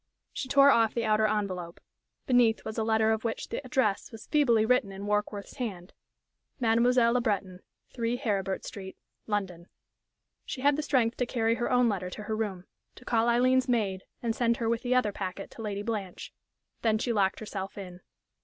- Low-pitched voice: No, high, 220 Hz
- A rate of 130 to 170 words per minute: No, average, 190 wpm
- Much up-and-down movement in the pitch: No, average, 3.2 semitones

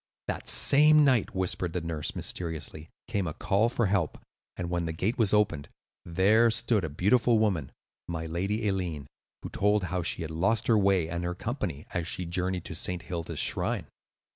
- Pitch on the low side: Yes, very low, 90 Hz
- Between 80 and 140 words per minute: No, average, 185 wpm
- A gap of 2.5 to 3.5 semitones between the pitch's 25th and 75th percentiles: No, average, 4.1 semitones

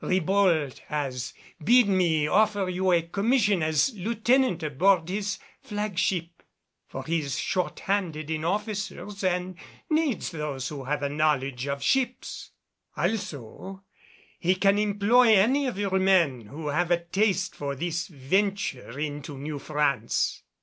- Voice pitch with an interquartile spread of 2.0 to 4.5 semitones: No, average, 5.2 semitones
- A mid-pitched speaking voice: Yes, medium, 180 Hz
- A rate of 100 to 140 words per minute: Yes, slow, 135 wpm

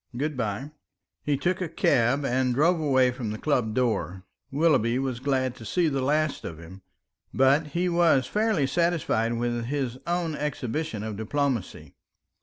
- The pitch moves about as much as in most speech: Yes, average, 4.5 semitones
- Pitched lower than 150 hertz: Yes, low, 135 Hz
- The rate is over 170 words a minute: No, average, 160 wpm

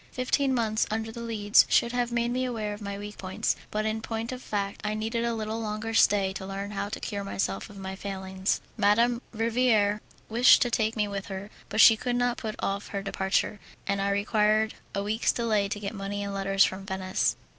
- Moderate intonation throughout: No, narrow, 2.2 semitones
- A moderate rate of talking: No, fast, 215 wpm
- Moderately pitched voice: No, high, 210 Hz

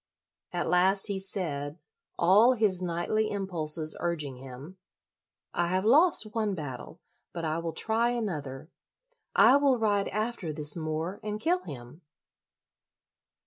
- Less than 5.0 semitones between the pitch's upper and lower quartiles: No, wide, 5.5 semitones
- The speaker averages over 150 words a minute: No, slow, 135 wpm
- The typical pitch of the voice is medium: Yes, medium, 180 Hz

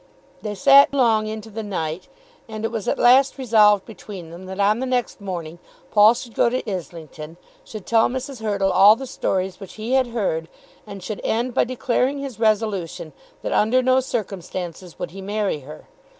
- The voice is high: Yes, high, 215 Hz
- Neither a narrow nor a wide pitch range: Yes, average, 4.3 semitones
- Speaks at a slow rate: No, average, 185 wpm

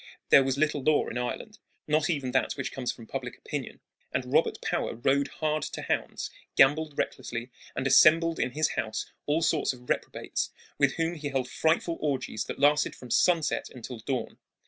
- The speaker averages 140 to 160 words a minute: No, average, 180 wpm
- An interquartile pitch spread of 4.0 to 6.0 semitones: No, average, 3.3 semitones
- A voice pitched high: No, medium, 140 Hz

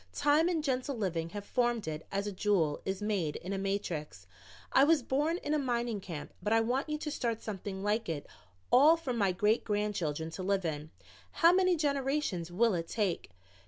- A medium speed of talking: Yes, average, 195 wpm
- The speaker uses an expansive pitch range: Yes, wide, 6.6 semitones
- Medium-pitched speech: No, high, 210 Hz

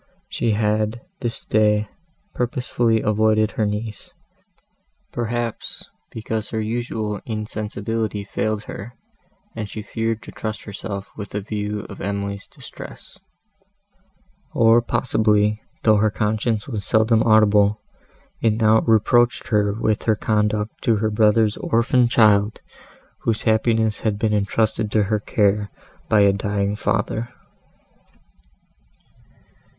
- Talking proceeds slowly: Yes, slow, 120 wpm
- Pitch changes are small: Yes, narrow, 1.3 semitones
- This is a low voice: Yes, low, 110 Hz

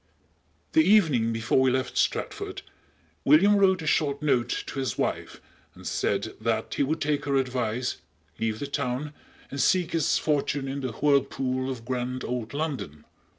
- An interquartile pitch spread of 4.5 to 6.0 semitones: No, average, 3.2 semitones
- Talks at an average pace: Yes, average, 165 wpm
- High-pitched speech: No, low, 135 Hz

